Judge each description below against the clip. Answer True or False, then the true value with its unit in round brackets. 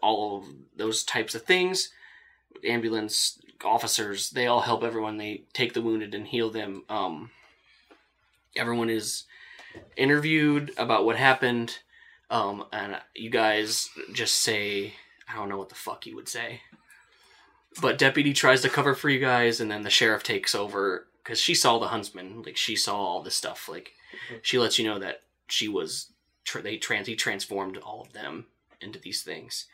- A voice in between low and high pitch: False (115 Hz)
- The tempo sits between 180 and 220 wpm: False (170 wpm)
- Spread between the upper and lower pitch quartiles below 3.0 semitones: False (4.0 semitones)